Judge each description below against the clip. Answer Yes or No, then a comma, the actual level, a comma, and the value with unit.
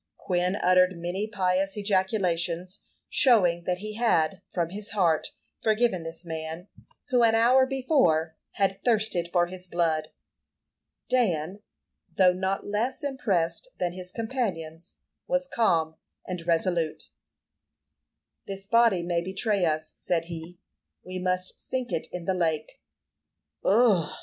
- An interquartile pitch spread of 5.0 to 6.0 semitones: No, average, 4.0 semitones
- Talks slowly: Yes, slow, 125 wpm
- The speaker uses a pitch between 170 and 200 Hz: Yes, medium, 185 Hz